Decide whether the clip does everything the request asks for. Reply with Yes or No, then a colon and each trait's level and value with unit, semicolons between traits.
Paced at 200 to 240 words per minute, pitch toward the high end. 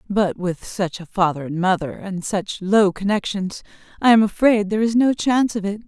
Yes: fast, 205 wpm; high, 200 Hz